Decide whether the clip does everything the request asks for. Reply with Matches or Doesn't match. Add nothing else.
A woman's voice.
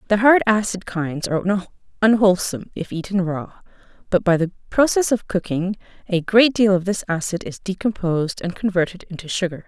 Matches